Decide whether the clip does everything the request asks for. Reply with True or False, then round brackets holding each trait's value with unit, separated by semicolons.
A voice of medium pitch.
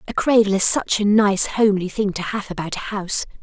False (200 Hz)